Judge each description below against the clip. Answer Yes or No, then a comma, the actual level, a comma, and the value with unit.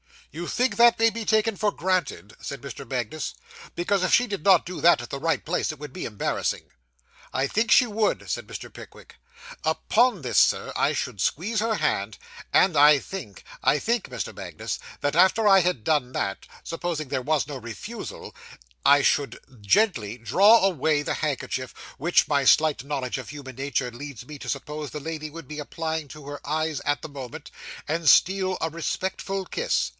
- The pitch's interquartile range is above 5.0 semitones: Yes, wide, 5.5 semitones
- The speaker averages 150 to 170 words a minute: No, average, 185 wpm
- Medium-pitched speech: Yes, medium, 155 Hz